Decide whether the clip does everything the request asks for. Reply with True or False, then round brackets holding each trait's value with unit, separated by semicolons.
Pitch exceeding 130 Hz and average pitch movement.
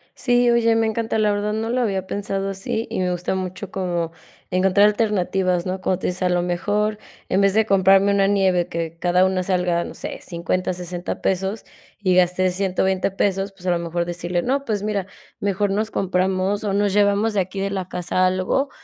False (190 Hz; 2.2 semitones)